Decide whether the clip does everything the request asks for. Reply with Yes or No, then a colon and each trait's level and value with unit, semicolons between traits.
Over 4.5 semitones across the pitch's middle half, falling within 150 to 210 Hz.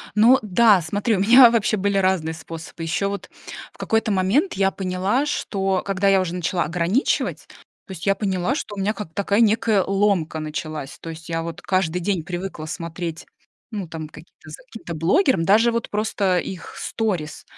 No: average, 4.0 semitones; high, 190 Hz